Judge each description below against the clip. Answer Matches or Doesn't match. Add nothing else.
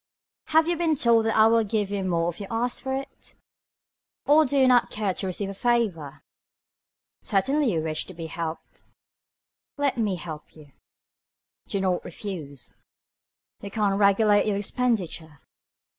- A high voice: Matches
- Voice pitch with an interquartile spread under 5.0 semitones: Doesn't match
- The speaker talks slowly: Doesn't match